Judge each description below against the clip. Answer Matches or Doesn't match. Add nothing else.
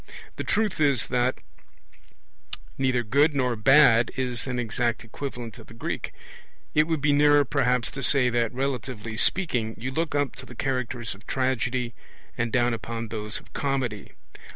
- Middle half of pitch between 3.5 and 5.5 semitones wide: Doesn't match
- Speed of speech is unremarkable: Matches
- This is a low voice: Matches